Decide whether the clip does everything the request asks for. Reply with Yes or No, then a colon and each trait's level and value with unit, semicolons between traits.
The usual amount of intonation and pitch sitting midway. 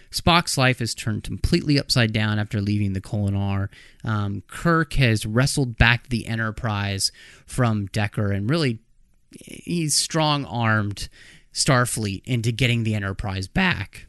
No: average, 4.1 semitones; low, 115 Hz